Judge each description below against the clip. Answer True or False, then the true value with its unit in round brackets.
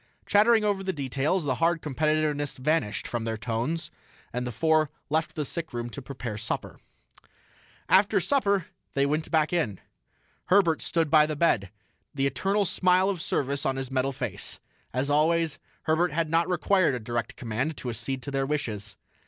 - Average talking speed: True (165 wpm)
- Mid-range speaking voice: True (150 Hz)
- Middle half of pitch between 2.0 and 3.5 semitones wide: False (4.7 semitones)